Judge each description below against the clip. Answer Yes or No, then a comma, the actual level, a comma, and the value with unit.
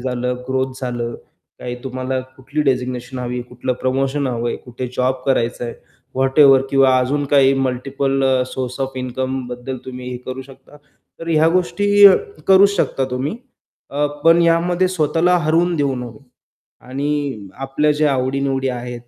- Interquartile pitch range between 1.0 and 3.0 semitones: Yes, narrow, 2.6 semitones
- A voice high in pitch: No, low, 130 Hz